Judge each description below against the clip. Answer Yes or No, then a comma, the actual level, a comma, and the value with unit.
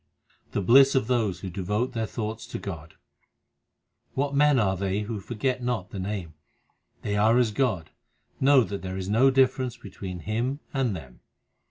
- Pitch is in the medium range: No, low, 110 Hz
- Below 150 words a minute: No, average, 175 wpm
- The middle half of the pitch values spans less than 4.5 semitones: No, average, 5.0 semitones